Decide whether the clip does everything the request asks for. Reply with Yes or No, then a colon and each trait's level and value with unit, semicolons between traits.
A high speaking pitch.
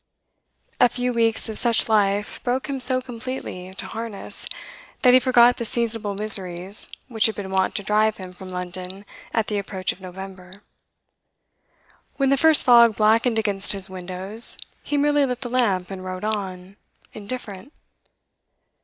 Yes: high, 215 Hz